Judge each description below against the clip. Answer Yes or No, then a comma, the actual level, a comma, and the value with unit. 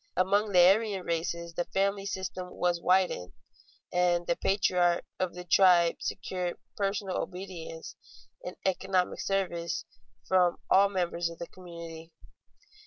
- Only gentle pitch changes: Yes, narrow, 2.0 semitones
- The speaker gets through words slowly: Yes, slow, 125 wpm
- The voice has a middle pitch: Yes, medium, 180 Hz